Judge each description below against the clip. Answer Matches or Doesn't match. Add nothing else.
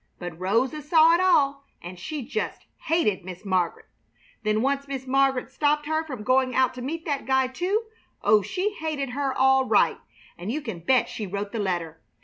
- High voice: Matches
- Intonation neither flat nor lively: Doesn't match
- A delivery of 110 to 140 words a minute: Doesn't match